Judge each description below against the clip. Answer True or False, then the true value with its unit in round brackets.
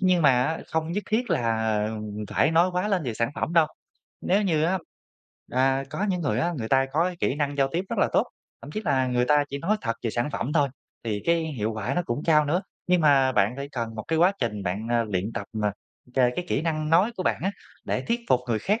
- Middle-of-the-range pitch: True (145 Hz)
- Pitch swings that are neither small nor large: False (6.4 semitones)